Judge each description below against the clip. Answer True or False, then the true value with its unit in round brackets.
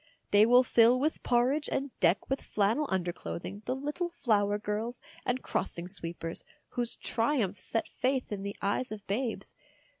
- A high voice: True (225 Hz)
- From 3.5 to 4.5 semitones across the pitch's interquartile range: True (4.2 semitones)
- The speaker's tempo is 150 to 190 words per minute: True (155 wpm)